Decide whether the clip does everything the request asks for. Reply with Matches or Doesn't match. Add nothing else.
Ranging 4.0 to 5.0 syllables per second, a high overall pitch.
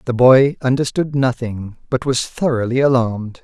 Doesn't match